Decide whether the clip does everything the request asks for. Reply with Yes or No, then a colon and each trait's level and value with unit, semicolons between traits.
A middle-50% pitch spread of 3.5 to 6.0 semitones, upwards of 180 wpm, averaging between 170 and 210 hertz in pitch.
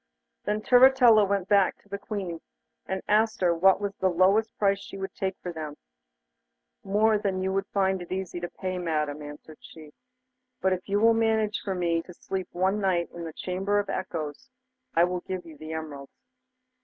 No: average, 3.0 semitones; average, 195 wpm; high, 190 Hz